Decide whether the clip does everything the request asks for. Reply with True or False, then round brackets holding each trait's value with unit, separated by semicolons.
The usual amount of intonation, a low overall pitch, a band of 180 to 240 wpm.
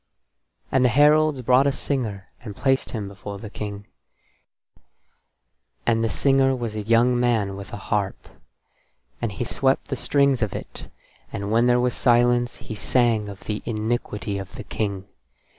False (3.5 semitones; 115 Hz; 160 wpm)